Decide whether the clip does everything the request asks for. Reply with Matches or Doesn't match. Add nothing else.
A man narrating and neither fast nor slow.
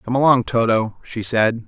Matches